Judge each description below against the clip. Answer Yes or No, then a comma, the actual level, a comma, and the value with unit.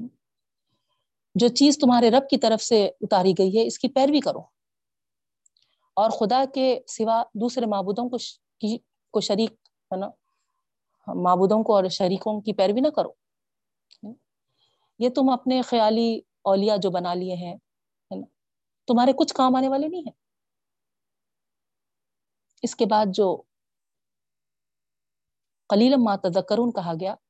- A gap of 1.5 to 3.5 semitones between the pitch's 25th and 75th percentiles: No, average, 4.1 semitones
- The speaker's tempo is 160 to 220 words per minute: No, average, 130 wpm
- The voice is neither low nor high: No, high, 225 Hz